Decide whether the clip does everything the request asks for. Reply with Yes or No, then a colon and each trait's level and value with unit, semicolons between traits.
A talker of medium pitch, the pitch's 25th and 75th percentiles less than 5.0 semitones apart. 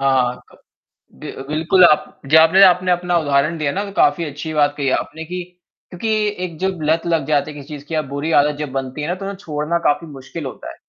Yes: medium, 155 Hz; average, 3.2 semitones